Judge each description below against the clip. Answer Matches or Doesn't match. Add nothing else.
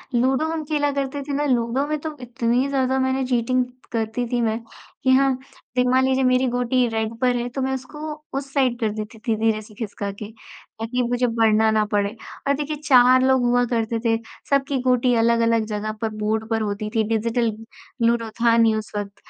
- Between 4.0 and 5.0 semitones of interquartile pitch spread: Doesn't match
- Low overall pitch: Doesn't match